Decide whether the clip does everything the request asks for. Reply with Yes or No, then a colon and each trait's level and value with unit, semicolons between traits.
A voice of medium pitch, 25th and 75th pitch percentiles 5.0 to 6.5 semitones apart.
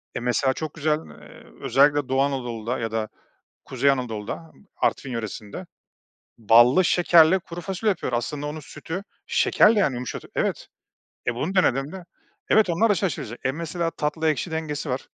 Yes: medium, 145 Hz; average, 5.3 semitones